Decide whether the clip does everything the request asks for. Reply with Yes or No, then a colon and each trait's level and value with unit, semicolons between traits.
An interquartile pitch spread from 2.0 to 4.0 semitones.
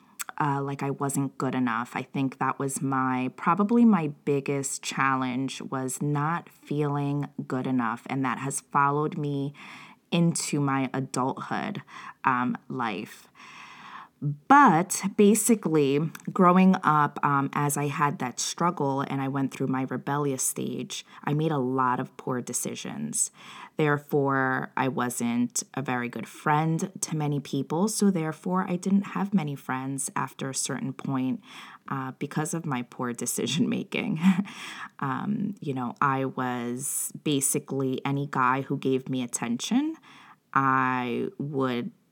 No: average, 4.7 semitones